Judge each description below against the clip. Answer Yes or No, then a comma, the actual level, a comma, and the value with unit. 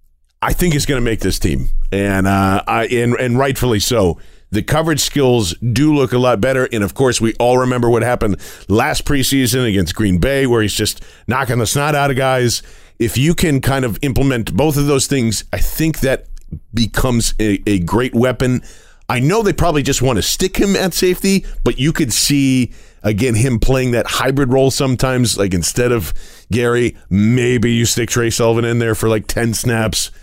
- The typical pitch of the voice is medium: No, low, 120 Hz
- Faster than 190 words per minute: Yes, average, 200 wpm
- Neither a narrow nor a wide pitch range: Yes, average, 3.8 semitones